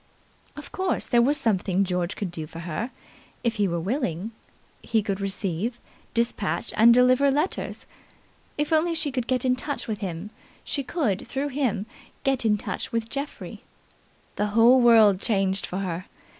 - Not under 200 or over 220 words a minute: No, average, 165 wpm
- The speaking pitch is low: No, high, 225 Hz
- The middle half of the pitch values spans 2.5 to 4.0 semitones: No, average, 5.2 semitones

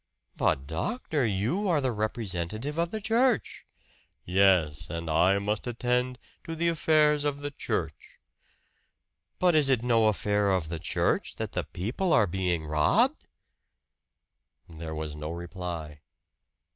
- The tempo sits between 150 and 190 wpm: No, slow, 135 wpm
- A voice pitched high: No, low, 105 Hz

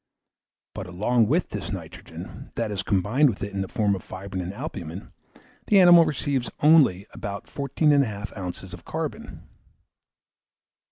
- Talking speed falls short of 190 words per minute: Yes, average, 150 wpm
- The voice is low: Yes, low, 105 Hz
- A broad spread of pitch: Yes, wide, 6.6 semitones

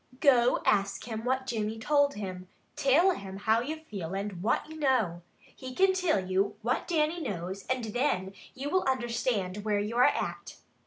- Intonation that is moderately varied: No, wide, 5.7 semitones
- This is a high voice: Yes, high, 230 Hz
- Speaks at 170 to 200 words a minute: Yes, average, 175 wpm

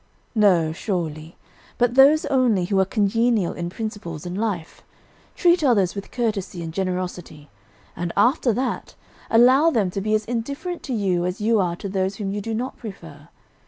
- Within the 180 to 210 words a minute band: No, average, 170 wpm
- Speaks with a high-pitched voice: Yes, high, 205 Hz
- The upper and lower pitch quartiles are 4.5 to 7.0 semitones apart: Yes, average, 4.9 semitones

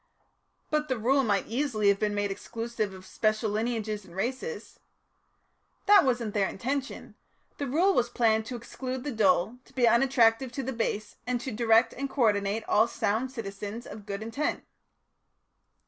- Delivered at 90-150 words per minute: No, average, 165 wpm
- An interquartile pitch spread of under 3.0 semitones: No, average, 3.6 semitones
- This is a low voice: No, high, 230 Hz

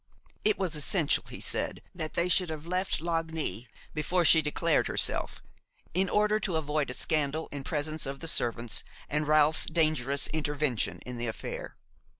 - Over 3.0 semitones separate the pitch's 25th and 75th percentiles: No, average, 2.7 semitones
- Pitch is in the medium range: Yes, medium, 155 Hz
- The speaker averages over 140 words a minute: Yes, average, 160 wpm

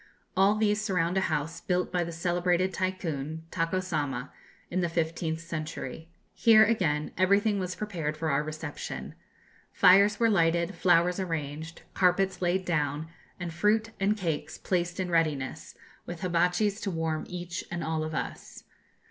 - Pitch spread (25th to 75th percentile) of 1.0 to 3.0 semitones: Yes, average, 2.7 semitones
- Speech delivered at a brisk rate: No, average, 150 wpm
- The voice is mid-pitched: Yes, medium, 175 Hz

